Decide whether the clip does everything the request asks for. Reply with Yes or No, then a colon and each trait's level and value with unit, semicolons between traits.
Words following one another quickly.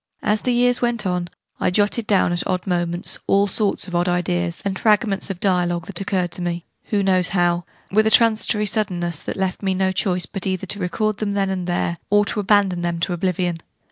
Yes: fast, 215 wpm